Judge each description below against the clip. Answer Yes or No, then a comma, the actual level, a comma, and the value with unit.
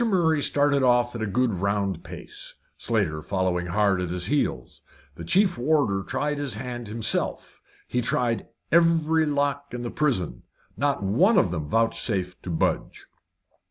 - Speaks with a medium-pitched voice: No, low, 120 Hz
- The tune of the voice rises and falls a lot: Yes, wide, 7.0 semitones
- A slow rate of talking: No, average, 155 wpm